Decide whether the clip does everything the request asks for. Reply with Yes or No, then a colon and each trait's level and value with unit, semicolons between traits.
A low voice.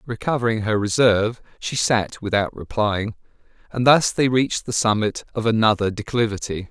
Yes: low, 110 Hz